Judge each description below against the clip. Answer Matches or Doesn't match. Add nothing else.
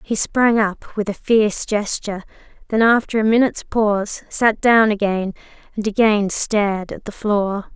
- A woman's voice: Matches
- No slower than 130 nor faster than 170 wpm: Matches